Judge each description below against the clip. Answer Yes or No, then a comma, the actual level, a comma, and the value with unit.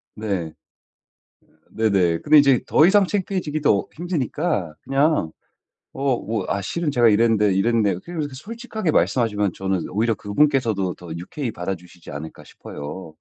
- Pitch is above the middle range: No, low, 115 Hz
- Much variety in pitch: Yes, wide, 7.7 semitones